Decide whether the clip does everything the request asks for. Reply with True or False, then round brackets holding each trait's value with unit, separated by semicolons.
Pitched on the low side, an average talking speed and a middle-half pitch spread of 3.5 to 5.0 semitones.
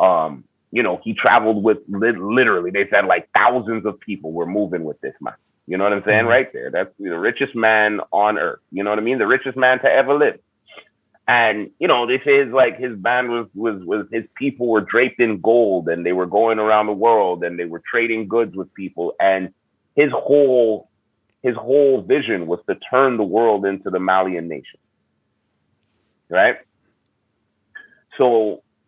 True (110 Hz; 185 wpm; 4.0 semitones)